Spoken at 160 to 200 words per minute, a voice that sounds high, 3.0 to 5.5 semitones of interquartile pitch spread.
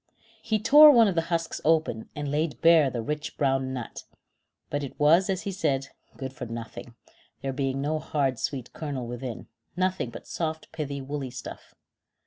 No: average, 175 wpm; medium, 145 Hz; average, 3.8 semitones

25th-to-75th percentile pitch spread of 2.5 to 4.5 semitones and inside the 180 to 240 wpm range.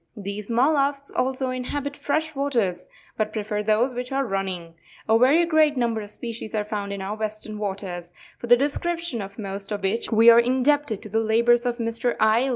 Yes: average, 4.1 semitones; average, 200 wpm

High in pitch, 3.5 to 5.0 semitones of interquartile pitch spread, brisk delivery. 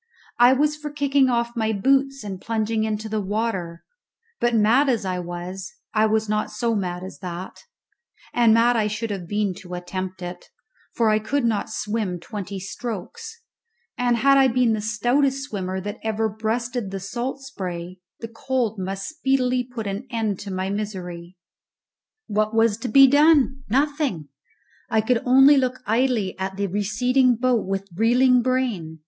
No: high, 220 Hz; average, 4.5 semitones; average, 165 wpm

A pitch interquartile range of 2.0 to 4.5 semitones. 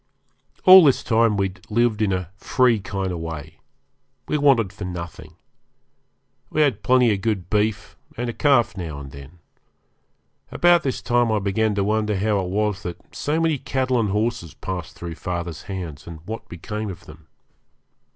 No: average, 5.0 semitones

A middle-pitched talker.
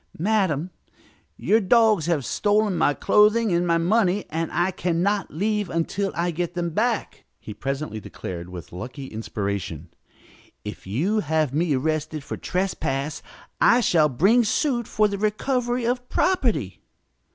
Yes: medium, 175 Hz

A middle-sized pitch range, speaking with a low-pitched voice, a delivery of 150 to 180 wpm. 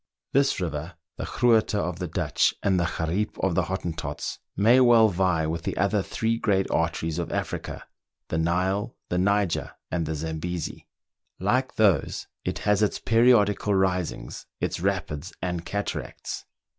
Yes: average, 3.8 semitones; very low, 95 Hz; average, 155 wpm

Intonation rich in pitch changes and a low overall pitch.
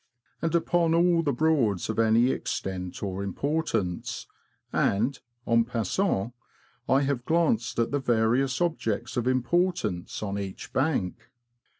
Yes: wide, 6.7 semitones; low, 120 Hz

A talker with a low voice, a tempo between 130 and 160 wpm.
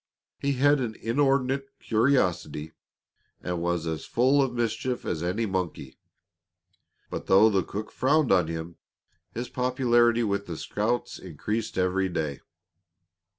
Yes: low, 110 Hz; slow, 135 wpm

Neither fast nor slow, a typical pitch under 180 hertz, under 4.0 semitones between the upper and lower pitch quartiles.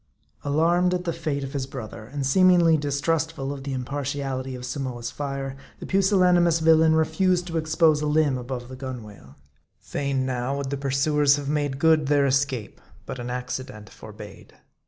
Yes: average, 170 wpm; medium, 140 Hz; average, 3.4 semitones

